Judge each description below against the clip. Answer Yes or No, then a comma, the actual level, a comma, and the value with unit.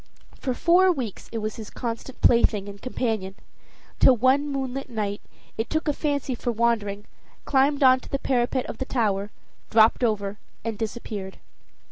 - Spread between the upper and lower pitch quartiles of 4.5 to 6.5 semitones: No, average, 3.9 semitones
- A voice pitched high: Yes, high, 235 Hz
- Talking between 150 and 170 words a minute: Yes, average, 160 wpm